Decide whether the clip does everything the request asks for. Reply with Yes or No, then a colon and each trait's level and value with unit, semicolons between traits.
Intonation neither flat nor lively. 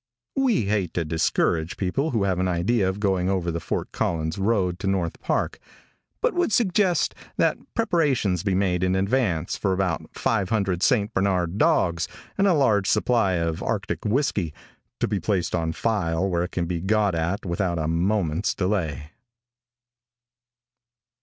Yes: average, 3.9 semitones